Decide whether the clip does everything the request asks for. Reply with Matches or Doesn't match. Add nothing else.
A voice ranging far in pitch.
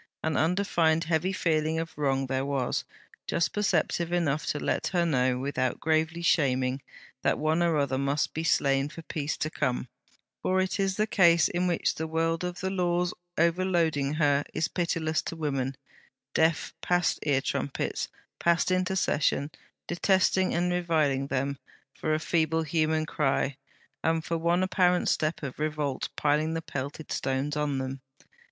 Doesn't match